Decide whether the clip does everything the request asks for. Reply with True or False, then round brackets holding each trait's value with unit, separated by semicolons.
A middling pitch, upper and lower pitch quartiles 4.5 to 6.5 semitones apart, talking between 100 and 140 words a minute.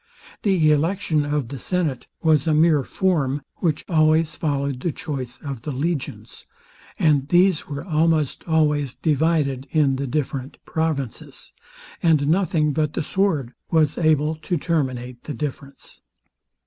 False (150 Hz; 2.7 semitones; 135 wpm)